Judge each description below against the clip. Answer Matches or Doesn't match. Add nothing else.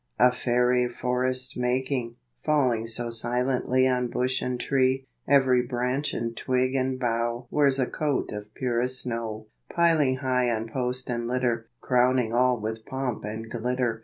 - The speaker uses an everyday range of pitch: Doesn't match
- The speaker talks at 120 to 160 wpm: Matches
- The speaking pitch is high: Doesn't match